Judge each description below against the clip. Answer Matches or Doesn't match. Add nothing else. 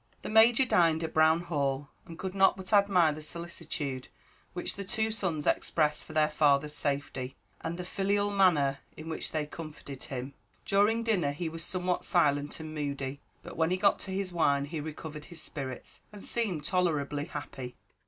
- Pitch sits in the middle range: Matches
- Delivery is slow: Doesn't match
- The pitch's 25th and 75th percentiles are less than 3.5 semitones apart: Doesn't match